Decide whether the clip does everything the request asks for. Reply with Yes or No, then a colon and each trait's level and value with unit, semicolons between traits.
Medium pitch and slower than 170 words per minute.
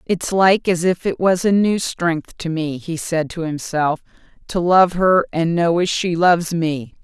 No: medium, 170 Hz; fast, 205 wpm